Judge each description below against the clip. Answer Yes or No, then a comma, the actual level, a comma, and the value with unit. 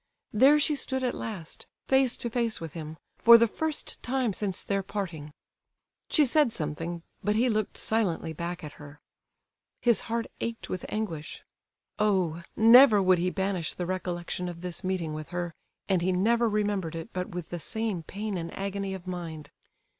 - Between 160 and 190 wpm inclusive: Yes, average, 175 wpm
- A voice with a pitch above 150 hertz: Yes, high, 190 Hz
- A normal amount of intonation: Yes, average, 4.7 semitones